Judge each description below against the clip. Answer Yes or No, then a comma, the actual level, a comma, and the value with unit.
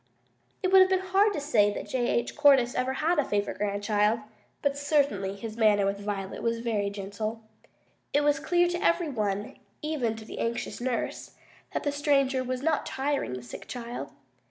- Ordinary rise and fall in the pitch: No, wide, 5.8 semitones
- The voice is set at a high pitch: Yes, high, 245 Hz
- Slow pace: No, average, 180 wpm